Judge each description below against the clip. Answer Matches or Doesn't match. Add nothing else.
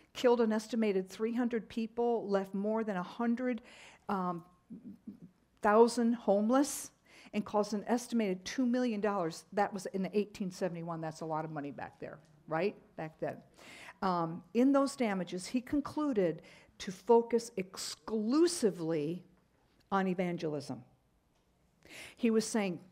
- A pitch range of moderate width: Matches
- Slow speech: Matches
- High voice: Matches